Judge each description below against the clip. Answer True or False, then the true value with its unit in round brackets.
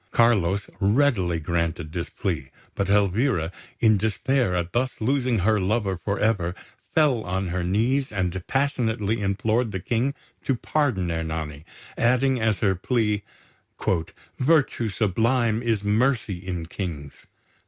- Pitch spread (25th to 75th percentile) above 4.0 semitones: True (4.9 semitones)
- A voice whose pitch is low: True (105 Hz)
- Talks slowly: True (130 wpm)